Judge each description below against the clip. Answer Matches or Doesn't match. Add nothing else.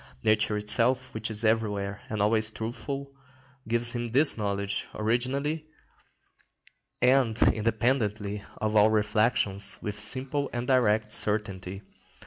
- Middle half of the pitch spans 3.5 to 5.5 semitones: Doesn't match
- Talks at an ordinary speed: Doesn't match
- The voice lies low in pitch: Matches